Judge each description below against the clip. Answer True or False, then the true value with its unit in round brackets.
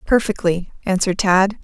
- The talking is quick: False (110 wpm)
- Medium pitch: False (195 Hz)